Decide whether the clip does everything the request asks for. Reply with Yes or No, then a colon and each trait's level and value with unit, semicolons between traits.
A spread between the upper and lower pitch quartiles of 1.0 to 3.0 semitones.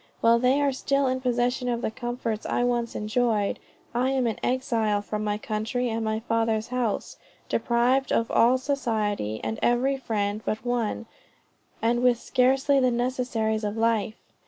Yes: narrow, 2.5 semitones